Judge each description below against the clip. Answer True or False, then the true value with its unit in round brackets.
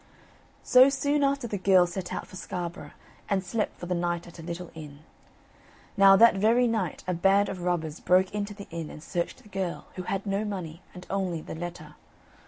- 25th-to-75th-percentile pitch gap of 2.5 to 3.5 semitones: True (2.8 semitones)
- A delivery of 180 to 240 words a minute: True (200 wpm)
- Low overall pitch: False (185 Hz)